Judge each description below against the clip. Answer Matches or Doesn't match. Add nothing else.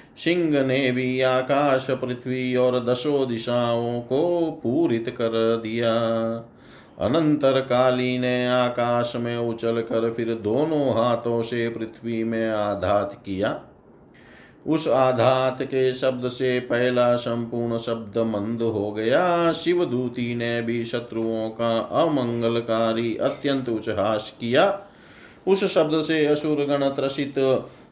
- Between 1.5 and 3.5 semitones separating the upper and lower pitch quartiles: Matches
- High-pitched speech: Doesn't match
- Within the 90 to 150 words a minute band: Matches